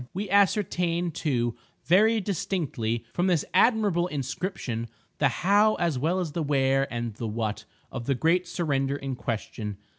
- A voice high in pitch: No, medium, 150 Hz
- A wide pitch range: Yes, wide, 6.9 semitones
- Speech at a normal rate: Yes, average, 150 wpm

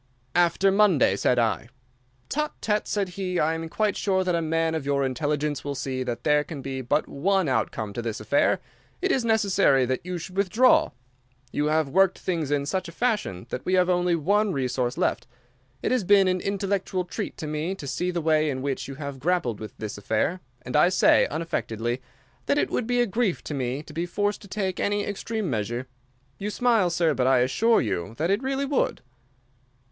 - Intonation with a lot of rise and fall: Yes, wide, 6.6 semitones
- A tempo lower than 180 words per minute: No, fast, 205 wpm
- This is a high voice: No, medium, 165 Hz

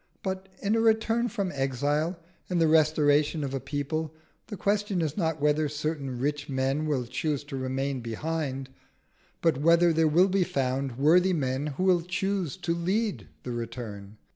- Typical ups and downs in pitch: Yes, average, 4.6 semitones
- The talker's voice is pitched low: No, medium, 150 Hz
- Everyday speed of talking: Yes, average, 165 wpm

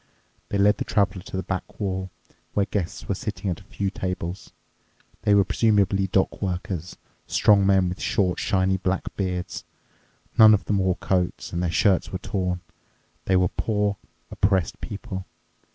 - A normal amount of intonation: No, narrow, 1.7 semitones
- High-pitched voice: No, very low, 95 Hz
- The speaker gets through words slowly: No, average, 165 wpm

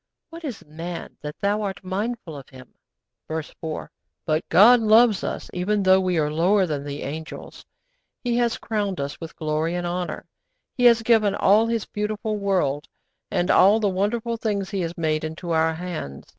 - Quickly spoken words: No, average, 180 wpm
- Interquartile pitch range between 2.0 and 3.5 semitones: No, average, 4.9 semitones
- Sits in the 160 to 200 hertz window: Yes, medium, 185 Hz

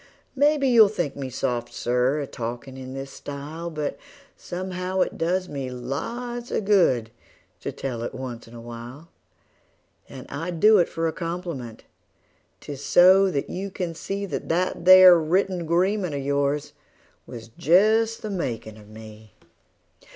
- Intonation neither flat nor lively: No, wide, 6.3 semitones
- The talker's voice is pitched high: No, medium, 160 Hz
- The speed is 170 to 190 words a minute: No, average, 155 wpm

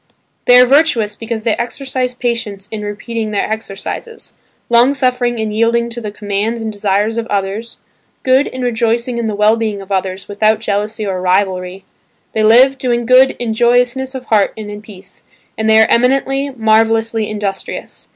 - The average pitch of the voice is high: Yes, high, 225 Hz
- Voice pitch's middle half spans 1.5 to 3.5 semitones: Yes, average, 2.8 semitones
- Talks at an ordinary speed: Yes, average, 170 wpm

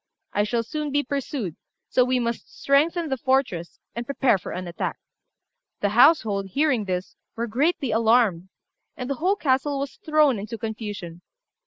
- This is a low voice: No, high, 245 Hz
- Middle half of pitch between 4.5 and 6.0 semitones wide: Yes, average, 5.1 semitones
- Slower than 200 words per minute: Yes, average, 160 wpm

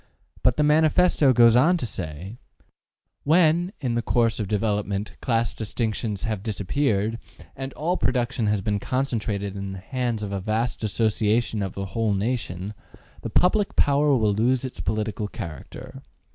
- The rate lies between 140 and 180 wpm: Yes, average, 160 wpm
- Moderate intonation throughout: Yes, average, 4.0 semitones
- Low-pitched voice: Yes, low, 115 Hz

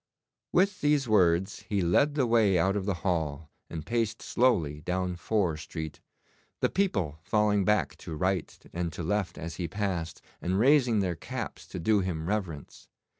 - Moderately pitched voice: No, very low, 95 Hz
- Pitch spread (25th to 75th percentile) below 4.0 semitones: No, average, 4.3 semitones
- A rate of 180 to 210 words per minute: No, average, 170 wpm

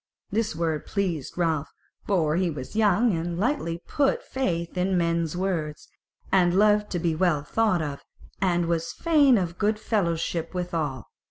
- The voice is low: No, medium, 175 Hz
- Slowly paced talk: No, average, 155 wpm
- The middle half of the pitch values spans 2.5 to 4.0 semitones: Yes, average, 3.7 semitones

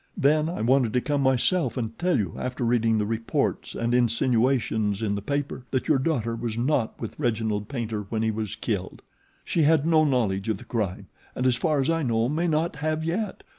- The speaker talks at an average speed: No, fast, 210 wpm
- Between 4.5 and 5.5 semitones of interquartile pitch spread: Yes, average, 4.9 semitones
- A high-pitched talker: No, low, 125 Hz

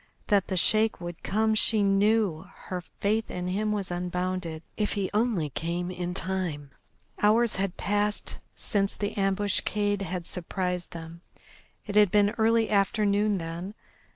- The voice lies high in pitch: Yes, high, 195 Hz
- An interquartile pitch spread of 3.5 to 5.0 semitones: No, average, 2.8 semitones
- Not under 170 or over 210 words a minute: No, average, 145 wpm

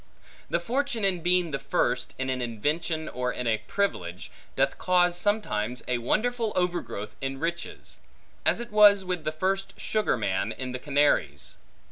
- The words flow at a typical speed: Yes, average, 160 wpm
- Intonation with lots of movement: Yes, wide, 7.6 semitones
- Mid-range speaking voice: Yes, medium, 155 Hz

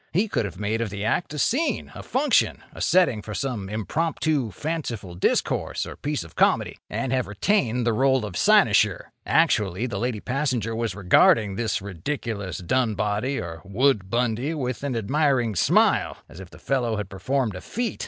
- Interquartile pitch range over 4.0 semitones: Yes, average, 5.2 semitones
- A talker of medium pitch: No, low, 115 Hz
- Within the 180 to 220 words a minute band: No, average, 170 wpm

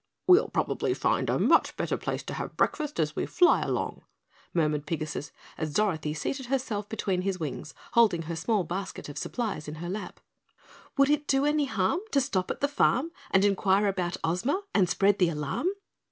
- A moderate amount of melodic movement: No, wide, 8.2 semitones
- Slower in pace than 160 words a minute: No, average, 185 wpm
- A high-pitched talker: Yes, high, 195 Hz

